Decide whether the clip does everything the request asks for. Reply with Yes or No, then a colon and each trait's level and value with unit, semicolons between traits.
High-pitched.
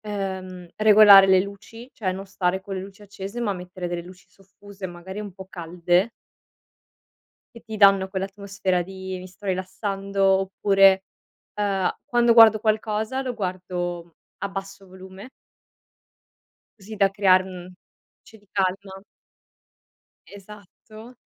Yes: high, 195 Hz